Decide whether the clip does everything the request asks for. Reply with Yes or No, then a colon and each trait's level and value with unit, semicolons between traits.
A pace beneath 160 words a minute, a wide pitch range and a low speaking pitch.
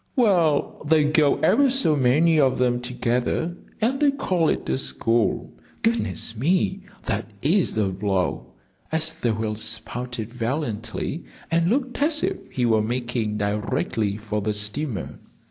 Yes: average, 145 wpm; wide, 7.1 semitones; low, 125 Hz